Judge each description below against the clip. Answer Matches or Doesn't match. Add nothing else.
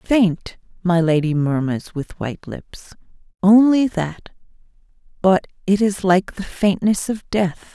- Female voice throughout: Matches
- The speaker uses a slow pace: Matches